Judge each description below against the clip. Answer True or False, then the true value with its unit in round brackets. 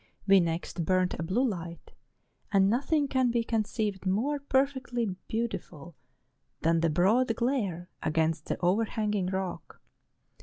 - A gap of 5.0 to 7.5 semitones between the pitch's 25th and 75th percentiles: True (5.3 semitones)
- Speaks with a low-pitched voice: False (200 Hz)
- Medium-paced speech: False (125 wpm)